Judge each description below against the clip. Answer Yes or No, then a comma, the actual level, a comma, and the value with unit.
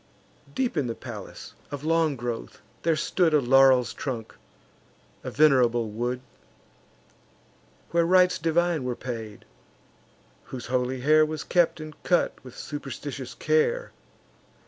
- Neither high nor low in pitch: Yes, medium, 145 Hz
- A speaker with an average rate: No, slow, 125 wpm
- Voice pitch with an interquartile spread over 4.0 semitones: Yes, average, 5.0 semitones